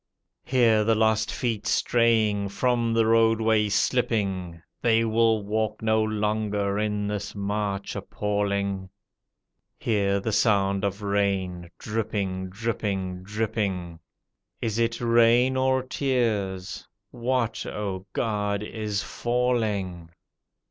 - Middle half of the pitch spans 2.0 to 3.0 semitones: Yes, narrow, 2.4 semitones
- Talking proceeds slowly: Yes, slow, 105 wpm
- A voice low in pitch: Yes, low, 105 Hz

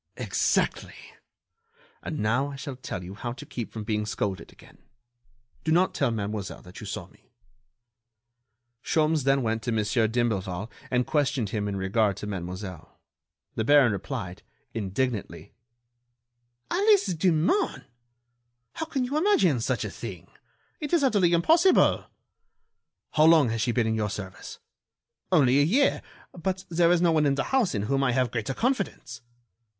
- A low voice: Yes, low, 125 Hz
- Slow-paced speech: No, average, 155 wpm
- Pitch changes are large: Yes, wide, 7.9 semitones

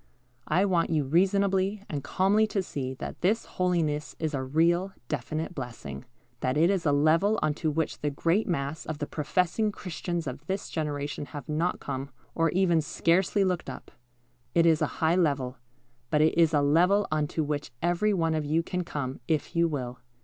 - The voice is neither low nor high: Yes, medium, 160 Hz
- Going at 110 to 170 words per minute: No, average, 190 wpm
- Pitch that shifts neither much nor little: Yes, average, 3.7 semitones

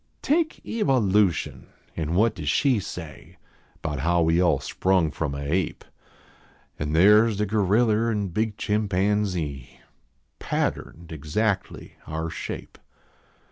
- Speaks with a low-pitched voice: Yes, very low, 95 Hz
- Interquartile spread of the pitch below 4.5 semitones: No, average, 4.8 semitones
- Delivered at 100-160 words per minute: Yes, slow, 135 wpm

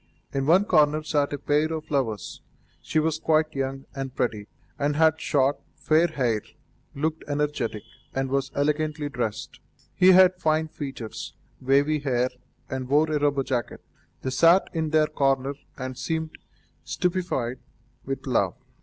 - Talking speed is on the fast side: No, average, 145 wpm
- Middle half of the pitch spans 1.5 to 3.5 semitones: Yes, average, 2.9 semitones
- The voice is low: No, medium, 145 Hz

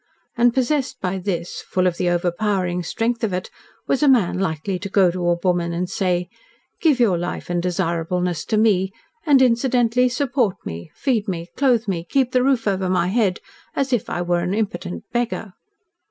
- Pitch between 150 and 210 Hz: Yes, high, 190 Hz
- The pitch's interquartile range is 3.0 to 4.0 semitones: No, average, 5.3 semitones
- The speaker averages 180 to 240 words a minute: Yes, average, 185 wpm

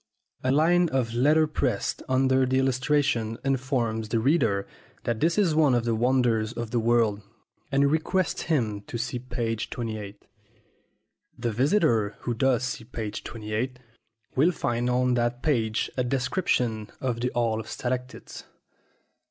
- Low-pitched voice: Yes, low, 125 Hz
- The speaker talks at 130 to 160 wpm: Yes, average, 145 wpm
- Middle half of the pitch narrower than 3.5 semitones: Yes, average, 3.0 semitones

